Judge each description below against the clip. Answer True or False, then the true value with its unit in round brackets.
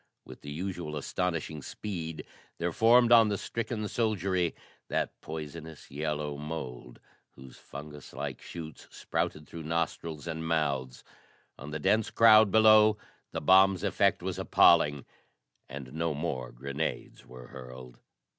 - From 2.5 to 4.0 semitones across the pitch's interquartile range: False (4.9 semitones)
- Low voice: True (80 Hz)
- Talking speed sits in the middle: False (130 wpm)